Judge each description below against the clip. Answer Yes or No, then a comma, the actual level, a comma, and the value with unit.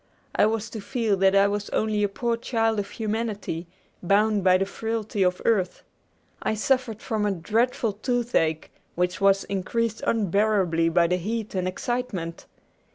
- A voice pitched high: Yes, high, 210 Hz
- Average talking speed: Yes, average, 160 wpm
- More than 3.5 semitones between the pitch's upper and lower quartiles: No, average, 3.2 semitones